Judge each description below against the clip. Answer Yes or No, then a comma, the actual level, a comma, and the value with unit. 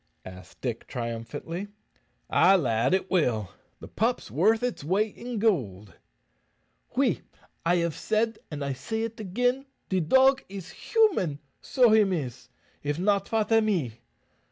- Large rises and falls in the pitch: Yes, wide, 8.3 semitones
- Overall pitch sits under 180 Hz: No, medium, 185 Hz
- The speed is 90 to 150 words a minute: Yes, average, 145 wpm